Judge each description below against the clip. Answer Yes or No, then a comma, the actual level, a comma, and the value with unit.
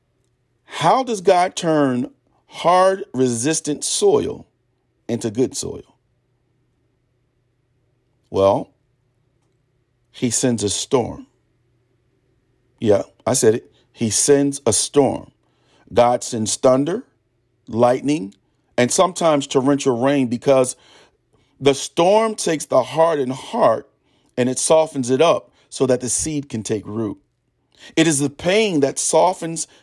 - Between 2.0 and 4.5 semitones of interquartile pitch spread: Yes, average, 3.0 semitones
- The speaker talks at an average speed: No, slow, 115 wpm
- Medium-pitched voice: No, low, 125 Hz